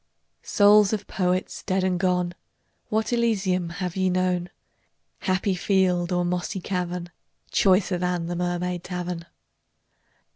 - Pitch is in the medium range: Yes, medium, 180 Hz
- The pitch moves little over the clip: Yes, narrow, 1.3 semitones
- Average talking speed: No, slow, 120 wpm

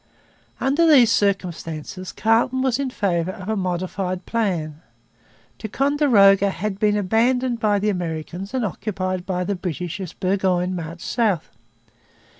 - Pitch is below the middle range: No, high, 195 Hz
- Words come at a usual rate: No, slow, 130 wpm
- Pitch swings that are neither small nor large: Yes, average, 3.8 semitones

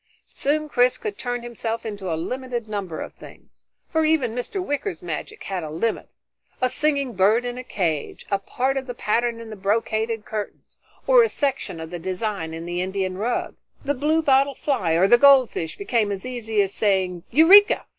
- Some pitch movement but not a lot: No, wide, 5.7 semitones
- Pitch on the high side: Yes, high, 230 Hz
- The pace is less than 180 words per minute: No, average, 185 wpm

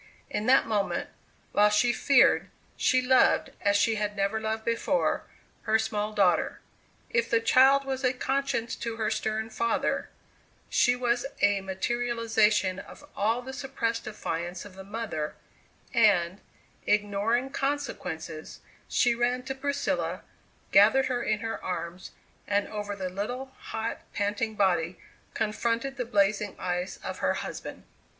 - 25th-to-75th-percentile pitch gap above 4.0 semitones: No, average, 3.3 semitones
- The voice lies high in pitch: Yes, high, 220 Hz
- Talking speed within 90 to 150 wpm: Yes, average, 140 wpm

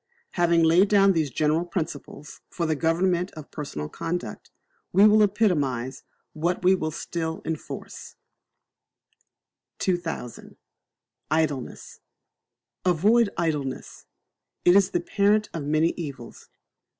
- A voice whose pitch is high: No, medium, 165 Hz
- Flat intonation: No, average, 3.3 semitones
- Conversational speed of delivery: No, slow, 110 wpm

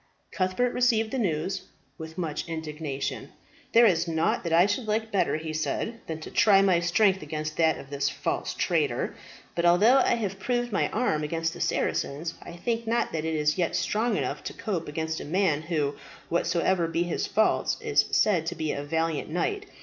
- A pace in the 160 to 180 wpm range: No, average, 195 wpm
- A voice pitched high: No, medium, 170 Hz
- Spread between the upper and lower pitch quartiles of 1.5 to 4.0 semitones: No, average, 5.0 semitones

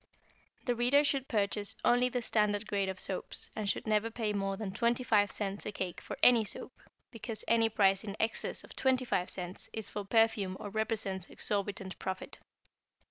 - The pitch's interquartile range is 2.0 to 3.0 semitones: Yes, narrow, 2.6 semitones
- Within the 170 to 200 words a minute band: Yes, average, 175 wpm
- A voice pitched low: No, high, 210 Hz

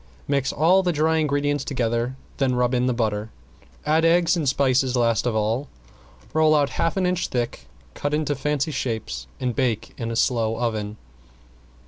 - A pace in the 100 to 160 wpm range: No, average, 170 wpm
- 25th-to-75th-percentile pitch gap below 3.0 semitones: No, average, 4.3 semitones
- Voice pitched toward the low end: Yes, low, 130 Hz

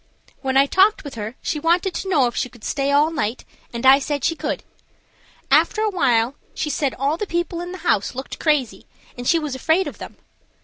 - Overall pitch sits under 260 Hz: No, very high, 285 Hz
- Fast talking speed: Yes, fast, 215 wpm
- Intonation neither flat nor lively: Yes, average, 4.7 semitones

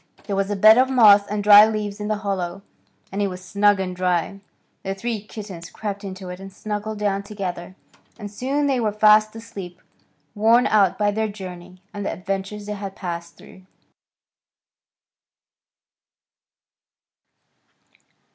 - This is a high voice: Yes, high, 205 Hz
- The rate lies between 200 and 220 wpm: No, average, 150 wpm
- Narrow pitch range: Yes, narrow, 1.9 semitones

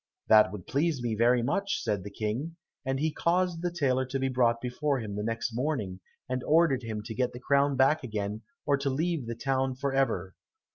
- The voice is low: Yes, low, 130 Hz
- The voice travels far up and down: No, average, 4.0 semitones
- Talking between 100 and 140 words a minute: No, fast, 205 wpm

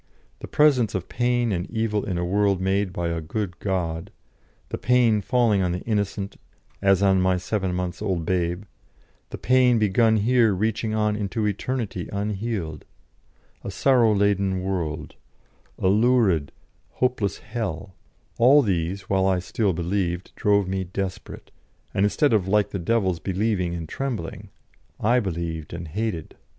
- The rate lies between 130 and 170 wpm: Yes, average, 150 wpm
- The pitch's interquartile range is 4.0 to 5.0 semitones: No, average, 3.6 semitones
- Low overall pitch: Yes, low, 100 Hz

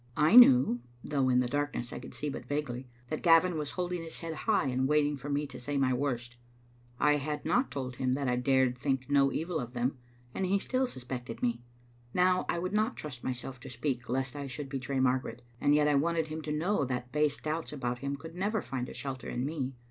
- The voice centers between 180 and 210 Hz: No, medium, 140 Hz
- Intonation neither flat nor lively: Yes, average, 3.4 semitones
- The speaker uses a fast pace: Yes, fast, 230 wpm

